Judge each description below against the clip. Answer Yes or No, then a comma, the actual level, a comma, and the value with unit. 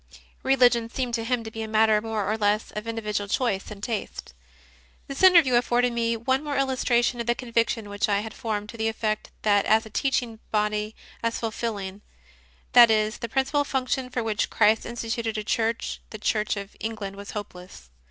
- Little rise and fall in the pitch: Yes, narrow, 2.2 semitones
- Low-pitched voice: No, high, 225 Hz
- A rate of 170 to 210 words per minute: Yes, average, 190 wpm